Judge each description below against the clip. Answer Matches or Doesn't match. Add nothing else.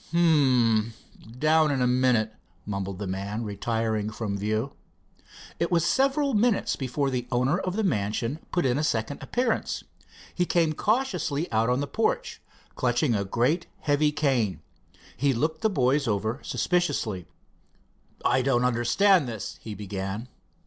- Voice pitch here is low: Matches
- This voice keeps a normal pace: Matches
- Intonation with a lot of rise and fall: Matches